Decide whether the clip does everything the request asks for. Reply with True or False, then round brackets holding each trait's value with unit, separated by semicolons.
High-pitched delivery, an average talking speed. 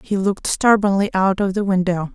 True (195 Hz; 195 wpm)